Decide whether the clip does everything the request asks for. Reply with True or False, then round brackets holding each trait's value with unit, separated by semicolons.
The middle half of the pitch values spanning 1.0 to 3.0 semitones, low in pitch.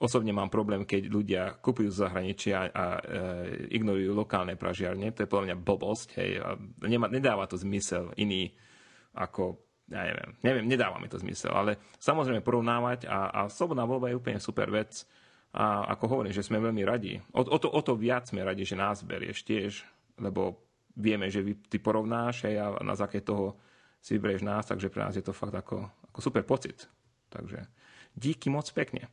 False (3.6 semitones; 105 Hz)